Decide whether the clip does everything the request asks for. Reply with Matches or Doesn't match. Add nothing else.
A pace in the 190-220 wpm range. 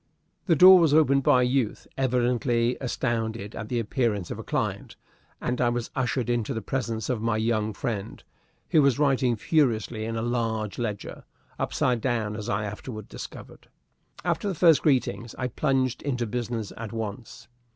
Doesn't match